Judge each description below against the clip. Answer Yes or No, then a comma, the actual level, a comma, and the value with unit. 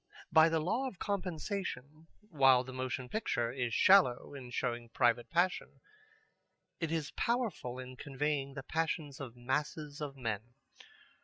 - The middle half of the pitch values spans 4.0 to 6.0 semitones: Yes, average, 4.6 semitones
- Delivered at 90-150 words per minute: Yes, average, 140 wpm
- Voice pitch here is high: No, medium, 140 Hz